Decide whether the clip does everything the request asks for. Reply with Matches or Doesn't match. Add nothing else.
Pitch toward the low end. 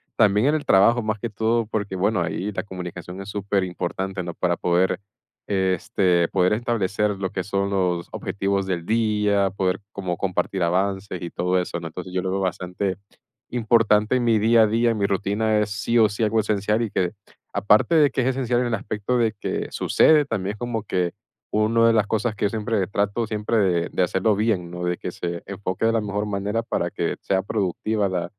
Matches